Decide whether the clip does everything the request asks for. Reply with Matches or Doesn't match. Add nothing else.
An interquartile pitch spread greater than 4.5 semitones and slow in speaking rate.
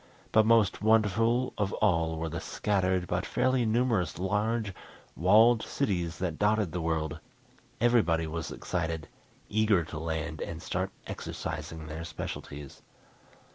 Matches